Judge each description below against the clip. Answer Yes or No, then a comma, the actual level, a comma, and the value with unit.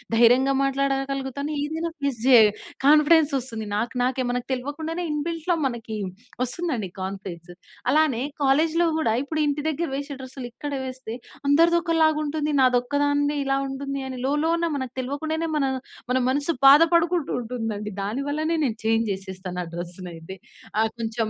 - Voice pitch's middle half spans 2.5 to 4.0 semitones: No, average, 4.9 semitones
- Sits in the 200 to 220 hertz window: No, very high, 275 Hz